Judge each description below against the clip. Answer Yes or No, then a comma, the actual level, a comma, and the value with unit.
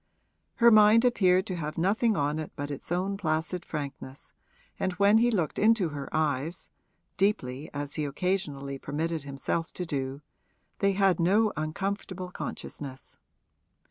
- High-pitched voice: No, medium, 170 Hz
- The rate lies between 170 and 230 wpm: No, average, 140 wpm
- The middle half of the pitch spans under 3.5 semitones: No, average, 5.3 semitones